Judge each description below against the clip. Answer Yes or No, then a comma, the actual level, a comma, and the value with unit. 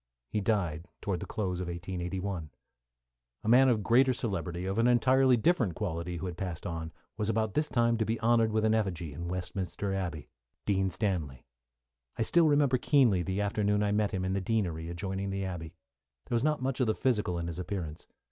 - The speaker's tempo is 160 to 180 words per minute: No, average, 200 wpm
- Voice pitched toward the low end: Yes, low, 100 Hz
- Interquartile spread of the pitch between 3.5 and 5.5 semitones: Yes, average, 4.4 semitones